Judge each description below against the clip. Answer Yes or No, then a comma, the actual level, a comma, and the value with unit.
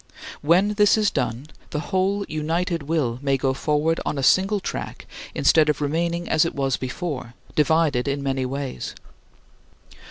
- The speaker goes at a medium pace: Yes, average, 155 wpm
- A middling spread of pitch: Yes, average, 4.0 semitones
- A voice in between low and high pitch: Yes, medium, 150 Hz